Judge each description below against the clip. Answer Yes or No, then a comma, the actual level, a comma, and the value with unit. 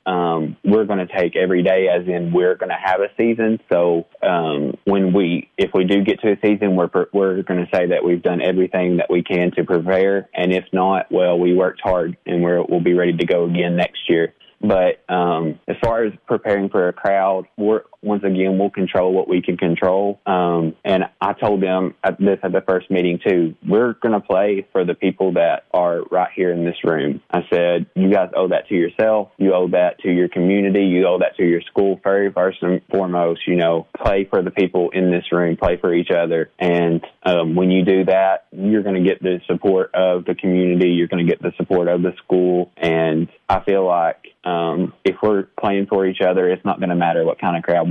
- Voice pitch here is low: Yes, very low, 90 Hz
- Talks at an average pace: No, fast, 225 wpm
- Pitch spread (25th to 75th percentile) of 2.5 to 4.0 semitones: No, narrow, 1.9 semitones